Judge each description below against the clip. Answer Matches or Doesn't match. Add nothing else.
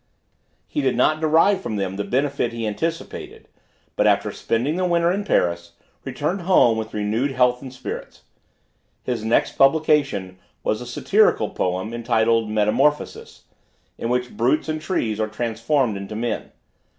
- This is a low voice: Matches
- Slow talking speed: Doesn't match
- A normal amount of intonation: Doesn't match